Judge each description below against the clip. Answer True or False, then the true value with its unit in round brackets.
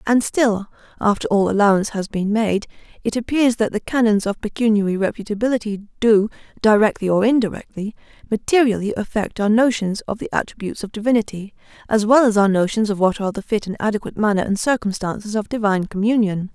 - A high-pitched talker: True (215 Hz)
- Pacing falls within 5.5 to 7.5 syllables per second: True (6.2 syllables/s)